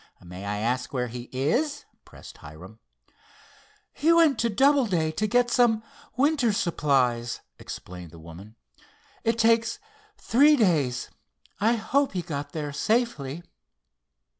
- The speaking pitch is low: No, medium, 170 Hz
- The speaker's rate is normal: No, slow, 125 wpm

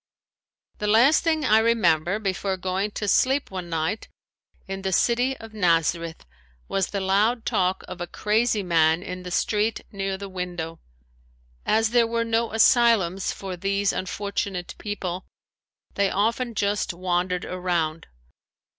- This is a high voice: Yes, high, 195 Hz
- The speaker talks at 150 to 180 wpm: No, average, 140 wpm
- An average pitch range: Yes, average, 3.6 semitones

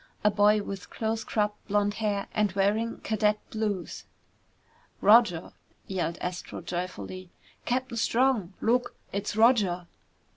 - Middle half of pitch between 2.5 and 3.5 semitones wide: Yes, average, 2.8 semitones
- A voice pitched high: Yes, high, 210 Hz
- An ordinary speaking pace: No, slow, 115 wpm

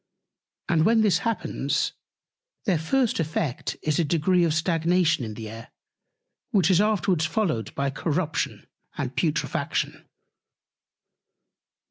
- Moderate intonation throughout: Yes, average, 3.8 semitones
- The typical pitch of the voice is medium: Yes, medium, 165 Hz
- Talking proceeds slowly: Yes, slow, 115 wpm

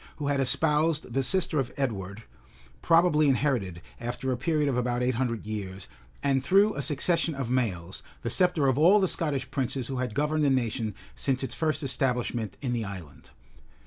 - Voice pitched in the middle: No, low, 130 Hz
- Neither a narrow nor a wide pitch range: Yes, average, 4.2 semitones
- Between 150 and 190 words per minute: Yes, average, 180 wpm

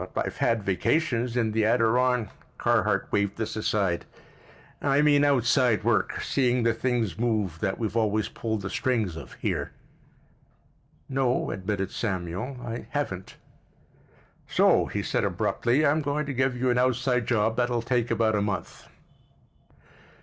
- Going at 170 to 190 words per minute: No, average, 145 wpm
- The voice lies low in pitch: Yes, low, 115 Hz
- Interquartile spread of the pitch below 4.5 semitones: Yes, average, 3.2 semitones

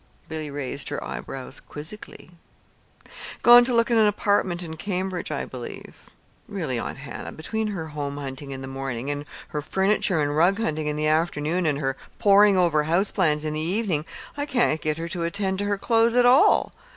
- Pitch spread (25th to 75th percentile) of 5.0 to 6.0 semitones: Yes, wide, 5.4 semitones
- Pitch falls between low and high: Yes, medium, 165 Hz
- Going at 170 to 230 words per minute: Yes, average, 190 wpm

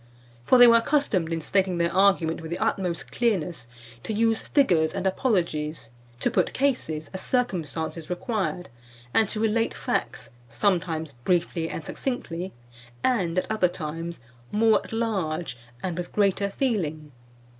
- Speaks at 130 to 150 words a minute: Yes, average, 145 wpm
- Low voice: No, medium, 185 Hz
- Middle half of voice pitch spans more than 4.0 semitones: Yes, average, 5.1 semitones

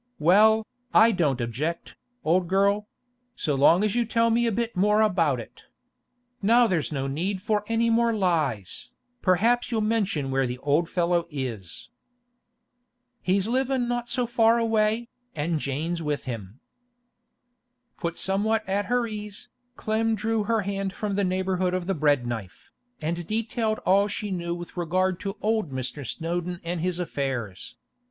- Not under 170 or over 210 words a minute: No, average, 155 wpm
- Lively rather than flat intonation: Yes, wide, 5.7 semitones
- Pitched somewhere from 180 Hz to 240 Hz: Yes, high, 190 Hz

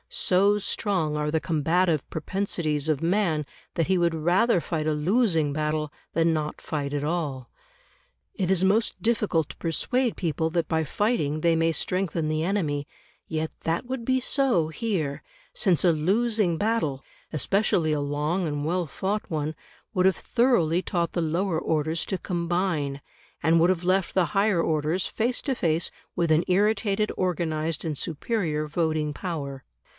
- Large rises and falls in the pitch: No, average, 3.8 semitones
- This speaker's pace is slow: No, average, 160 wpm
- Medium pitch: Yes, medium, 165 Hz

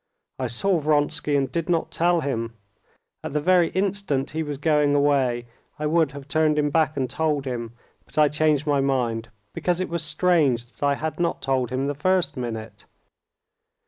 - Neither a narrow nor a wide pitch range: Yes, average, 3.2 semitones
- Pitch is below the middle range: No, medium, 145 Hz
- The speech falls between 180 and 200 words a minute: Yes, average, 185 wpm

